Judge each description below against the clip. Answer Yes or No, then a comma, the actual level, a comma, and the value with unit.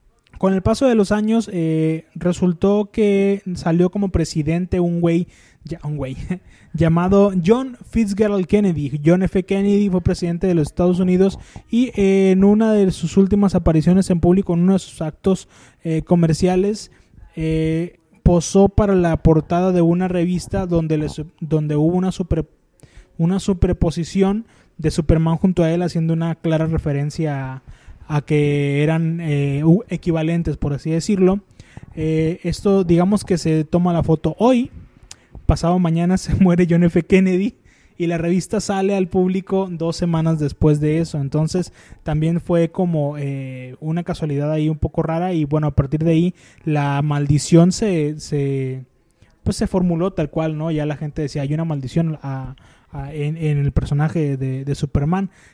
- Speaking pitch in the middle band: Yes, medium, 170 Hz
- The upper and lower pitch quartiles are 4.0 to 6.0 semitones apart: No, average, 3.2 semitones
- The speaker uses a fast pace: No, average, 165 wpm